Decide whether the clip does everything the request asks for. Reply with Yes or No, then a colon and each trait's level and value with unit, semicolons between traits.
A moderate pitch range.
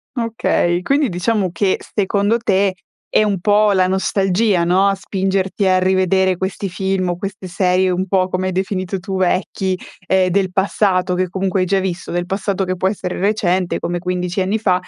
No: narrow, 1.3 semitones